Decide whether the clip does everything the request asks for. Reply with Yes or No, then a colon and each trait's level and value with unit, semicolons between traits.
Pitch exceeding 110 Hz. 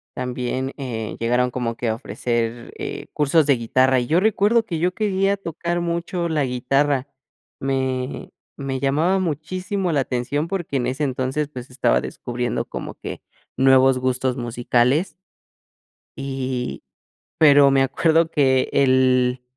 Yes: low, 135 Hz